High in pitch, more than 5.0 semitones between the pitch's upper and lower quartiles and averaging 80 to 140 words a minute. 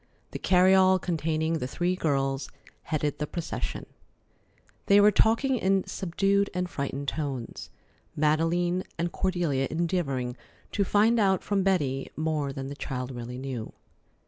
No: medium, 165 Hz; wide, 5.4 semitones; slow, 135 wpm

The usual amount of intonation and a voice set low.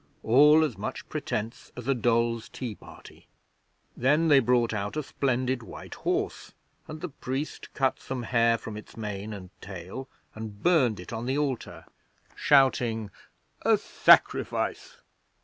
Yes: average, 3.5 semitones; low, 120 Hz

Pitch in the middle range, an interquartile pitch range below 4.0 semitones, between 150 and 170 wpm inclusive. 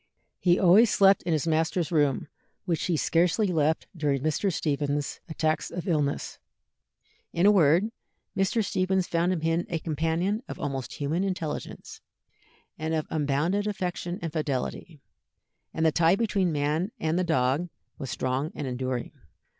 Yes: medium, 165 Hz; average, 3.5 semitones; average, 155 wpm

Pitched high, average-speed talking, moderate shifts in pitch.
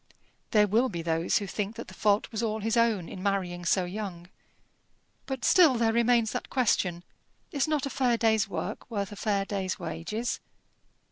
Yes: high, 215 Hz; average, 185 wpm; average, 3.8 semitones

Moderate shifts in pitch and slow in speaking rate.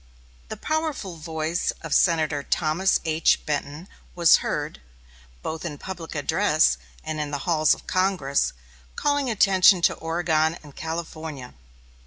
Yes: average, 3.1 semitones; slow, 130 wpm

